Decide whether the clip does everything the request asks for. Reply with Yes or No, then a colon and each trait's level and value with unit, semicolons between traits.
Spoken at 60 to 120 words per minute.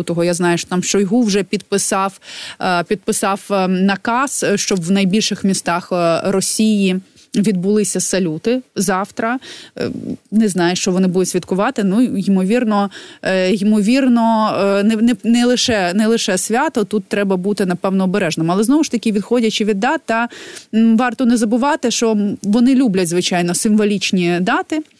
No: average, 135 wpm